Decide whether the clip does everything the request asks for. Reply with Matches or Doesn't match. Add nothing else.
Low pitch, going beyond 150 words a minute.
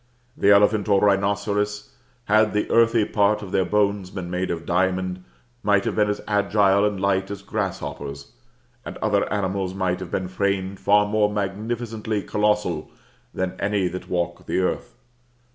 Matches